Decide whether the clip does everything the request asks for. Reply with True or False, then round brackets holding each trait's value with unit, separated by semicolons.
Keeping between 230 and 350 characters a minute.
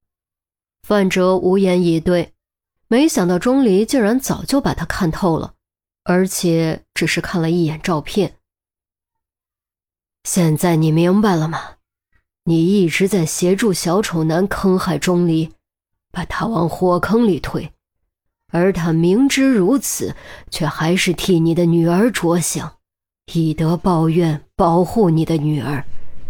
False (190 characters per minute)